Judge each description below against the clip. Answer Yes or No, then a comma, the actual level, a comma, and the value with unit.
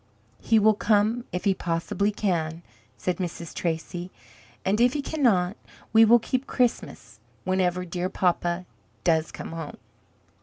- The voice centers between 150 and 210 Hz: Yes, medium, 185 Hz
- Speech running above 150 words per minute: No, average, 140 wpm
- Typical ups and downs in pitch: Yes, average, 3.9 semitones